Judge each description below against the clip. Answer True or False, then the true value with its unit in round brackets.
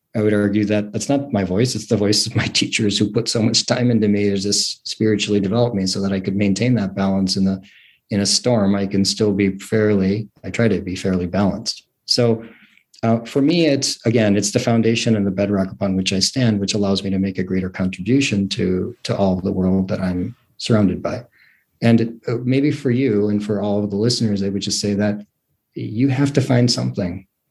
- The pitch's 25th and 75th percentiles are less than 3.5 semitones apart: True (2.9 semitones)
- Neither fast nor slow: False (230 wpm)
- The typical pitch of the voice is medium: False (105 Hz)